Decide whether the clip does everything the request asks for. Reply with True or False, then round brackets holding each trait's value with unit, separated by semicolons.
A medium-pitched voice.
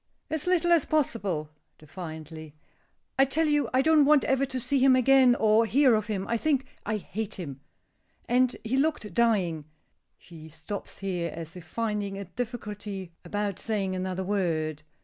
False (210 Hz)